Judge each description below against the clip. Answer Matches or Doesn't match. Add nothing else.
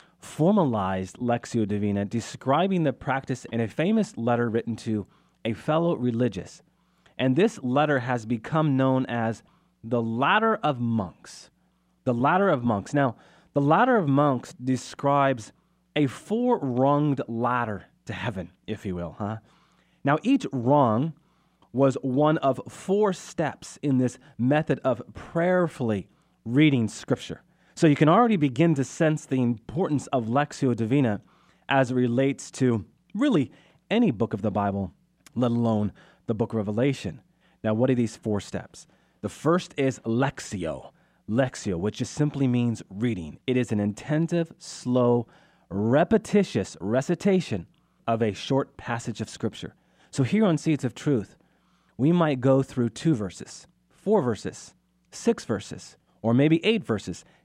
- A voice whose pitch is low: Matches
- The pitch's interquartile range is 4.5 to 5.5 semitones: Matches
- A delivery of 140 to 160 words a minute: Matches